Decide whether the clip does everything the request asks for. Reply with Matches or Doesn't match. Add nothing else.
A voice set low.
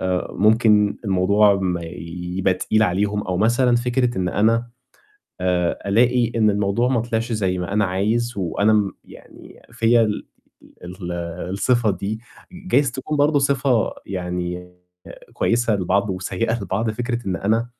Matches